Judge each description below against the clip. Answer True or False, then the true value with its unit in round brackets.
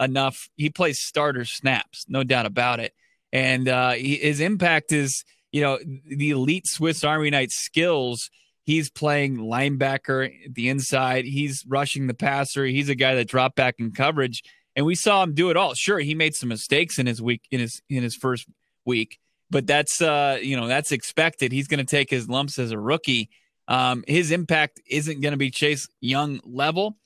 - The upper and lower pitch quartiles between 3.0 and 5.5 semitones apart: False (2.6 semitones)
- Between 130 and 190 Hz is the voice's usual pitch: True (140 Hz)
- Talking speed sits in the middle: True (190 wpm)